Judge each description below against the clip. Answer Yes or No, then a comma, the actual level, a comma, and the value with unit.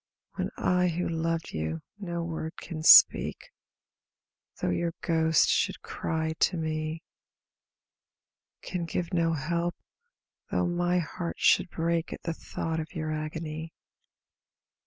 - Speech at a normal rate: No, slow, 125 wpm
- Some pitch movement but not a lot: No, narrow, 1.4 semitones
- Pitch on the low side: No, medium, 165 Hz